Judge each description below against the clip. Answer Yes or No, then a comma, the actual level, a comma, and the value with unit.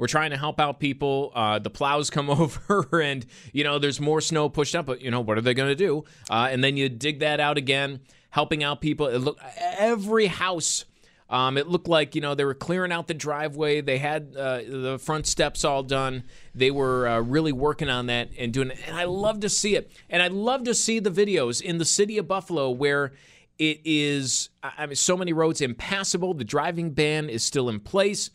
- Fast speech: Yes, fast, 225 wpm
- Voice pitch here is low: No, medium, 150 Hz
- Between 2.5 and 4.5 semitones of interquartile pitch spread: Yes, average, 4.0 semitones